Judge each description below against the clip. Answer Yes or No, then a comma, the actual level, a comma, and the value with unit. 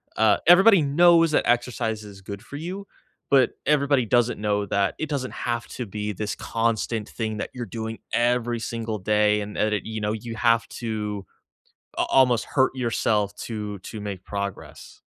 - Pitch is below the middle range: Yes, low, 115 Hz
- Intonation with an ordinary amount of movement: Yes, average, 3.0 semitones